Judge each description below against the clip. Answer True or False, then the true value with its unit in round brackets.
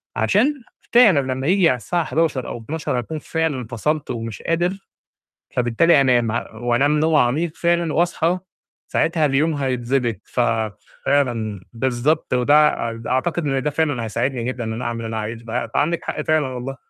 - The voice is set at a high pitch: False (135 Hz)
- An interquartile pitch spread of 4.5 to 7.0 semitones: True (5.0 semitones)